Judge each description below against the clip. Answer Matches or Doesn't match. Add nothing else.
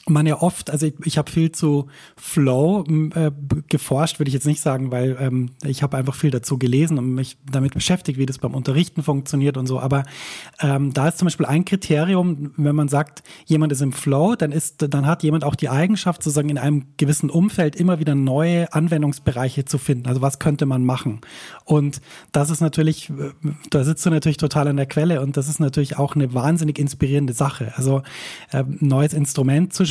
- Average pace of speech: Doesn't match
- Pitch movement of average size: Doesn't match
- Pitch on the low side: Doesn't match